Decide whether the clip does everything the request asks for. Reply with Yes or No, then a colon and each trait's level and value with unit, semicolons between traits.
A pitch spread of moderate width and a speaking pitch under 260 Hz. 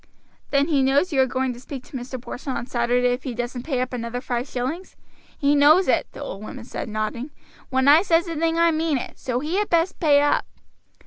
No: average, 4.0 semitones; very high, 265 Hz